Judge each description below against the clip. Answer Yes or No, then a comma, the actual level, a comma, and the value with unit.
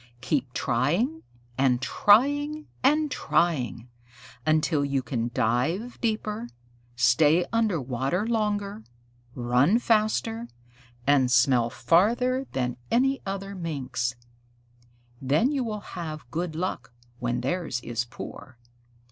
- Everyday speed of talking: No, slow, 105 wpm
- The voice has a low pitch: No, medium, 160 Hz